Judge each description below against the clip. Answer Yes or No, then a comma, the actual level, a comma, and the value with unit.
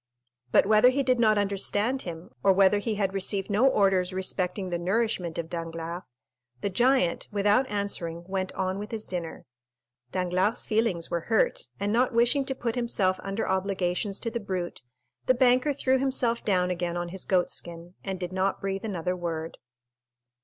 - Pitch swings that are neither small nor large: Yes, average, 3.9 semitones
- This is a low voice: No, high, 195 Hz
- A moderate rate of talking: Yes, average, 175 wpm